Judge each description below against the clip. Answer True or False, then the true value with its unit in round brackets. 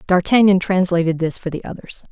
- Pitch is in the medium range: True (180 Hz)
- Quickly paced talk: False (170 wpm)